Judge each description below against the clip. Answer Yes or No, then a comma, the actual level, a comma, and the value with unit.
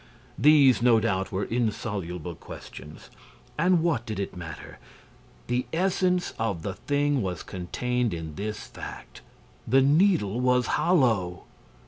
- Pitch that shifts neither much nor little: No, wide, 7.0 semitones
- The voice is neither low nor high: No, low, 115 Hz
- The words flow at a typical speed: No, slow, 125 wpm